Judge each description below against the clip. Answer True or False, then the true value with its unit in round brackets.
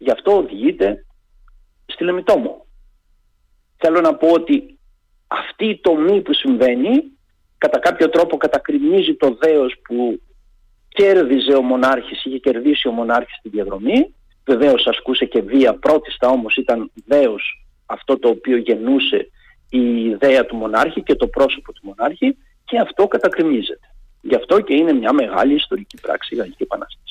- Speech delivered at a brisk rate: False (145 wpm)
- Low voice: False (165 Hz)